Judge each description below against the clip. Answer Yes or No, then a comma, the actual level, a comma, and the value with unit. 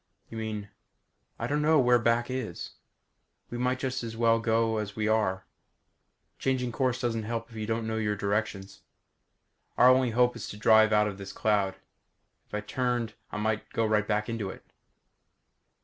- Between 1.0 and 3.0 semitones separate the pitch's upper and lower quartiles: Yes, narrow, 2.4 semitones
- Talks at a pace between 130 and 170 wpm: No, average, 185 wpm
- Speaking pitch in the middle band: No, low, 110 Hz